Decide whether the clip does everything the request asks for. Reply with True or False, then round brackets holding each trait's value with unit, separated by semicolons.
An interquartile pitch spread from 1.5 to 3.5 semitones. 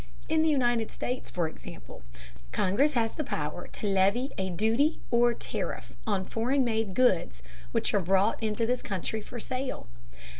False (4.7 semitones)